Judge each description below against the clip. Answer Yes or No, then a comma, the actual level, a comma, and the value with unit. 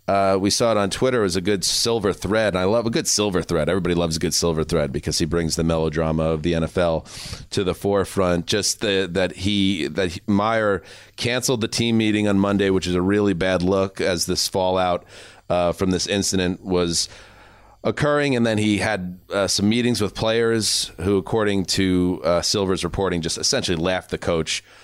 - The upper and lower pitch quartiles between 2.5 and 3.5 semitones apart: Yes, average, 2.9 semitones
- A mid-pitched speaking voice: No, very low, 95 Hz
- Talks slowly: No, average, 200 wpm